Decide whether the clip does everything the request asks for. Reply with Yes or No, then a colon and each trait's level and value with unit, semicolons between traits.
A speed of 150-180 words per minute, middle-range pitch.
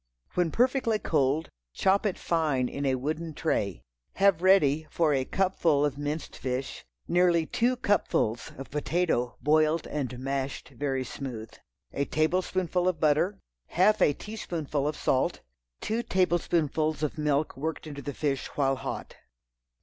No: average, 140 wpm; medium, 155 Hz